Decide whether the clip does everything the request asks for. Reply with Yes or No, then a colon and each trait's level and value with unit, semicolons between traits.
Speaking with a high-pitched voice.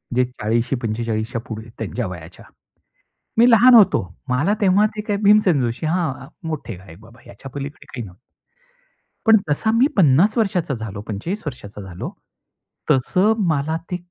No: low, 135 Hz